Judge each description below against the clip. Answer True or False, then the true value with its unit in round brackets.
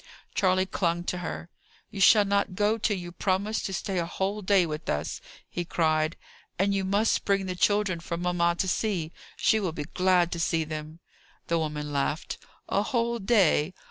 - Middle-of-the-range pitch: True (180 Hz)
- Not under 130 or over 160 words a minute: False (185 wpm)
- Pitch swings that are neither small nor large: True (3.3 semitones)